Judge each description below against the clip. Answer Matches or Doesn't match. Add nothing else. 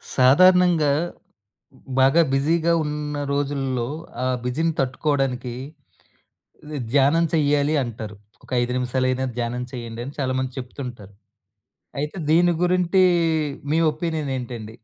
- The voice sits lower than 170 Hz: Matches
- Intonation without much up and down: Doesn't match